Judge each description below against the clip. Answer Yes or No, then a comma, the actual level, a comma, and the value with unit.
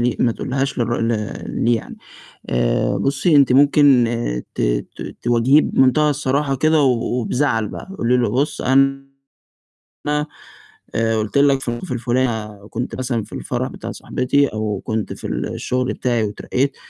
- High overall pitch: No, low, 125 Hz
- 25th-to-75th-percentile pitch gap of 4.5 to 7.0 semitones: No, average, 3.2 semitones